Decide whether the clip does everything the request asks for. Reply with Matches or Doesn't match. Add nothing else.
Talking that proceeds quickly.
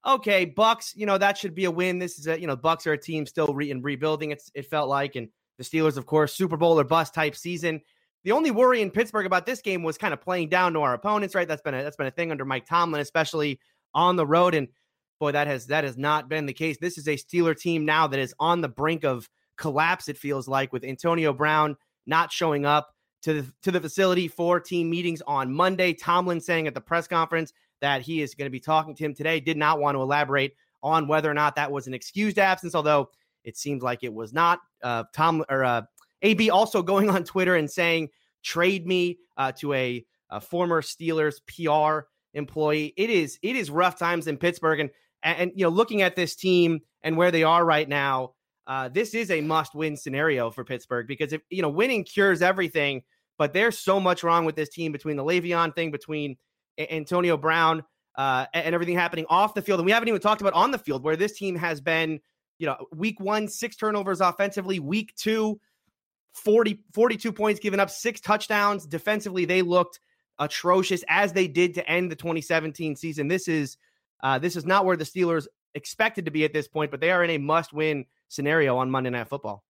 Matches